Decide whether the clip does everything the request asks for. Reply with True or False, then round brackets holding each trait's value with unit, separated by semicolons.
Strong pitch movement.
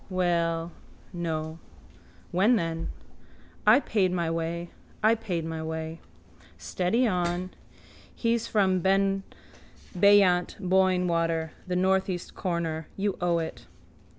False (2.6 semitones)